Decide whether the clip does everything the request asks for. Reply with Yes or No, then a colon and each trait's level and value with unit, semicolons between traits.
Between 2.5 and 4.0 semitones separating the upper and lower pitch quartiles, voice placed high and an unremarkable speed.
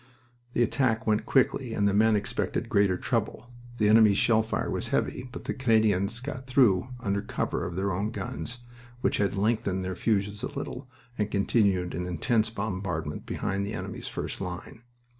No: average, 2.9 semitones; low, 105 Hz; average, 175 wpm